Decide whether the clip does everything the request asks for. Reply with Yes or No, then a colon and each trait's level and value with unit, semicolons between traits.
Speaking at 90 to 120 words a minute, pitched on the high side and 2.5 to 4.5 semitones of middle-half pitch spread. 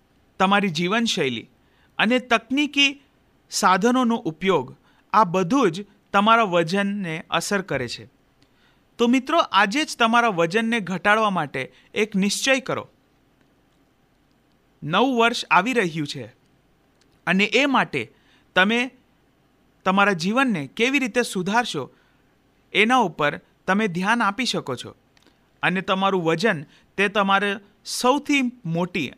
No: slow, 110 wpm; high, 200 Hz; wide, 5.5 semitones